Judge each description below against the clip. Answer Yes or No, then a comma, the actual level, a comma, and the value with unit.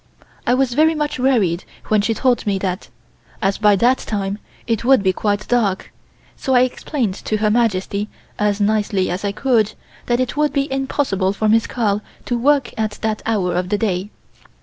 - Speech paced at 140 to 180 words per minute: No, average, 190 wpm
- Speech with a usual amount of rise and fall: Yes, average, 3.9 semitones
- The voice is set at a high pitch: Yes, high, 215 Hz